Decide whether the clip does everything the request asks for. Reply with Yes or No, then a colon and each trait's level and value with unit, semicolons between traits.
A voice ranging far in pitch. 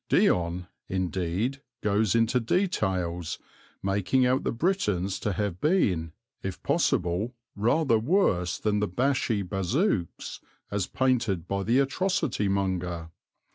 Yes: wide, 5.8 semitones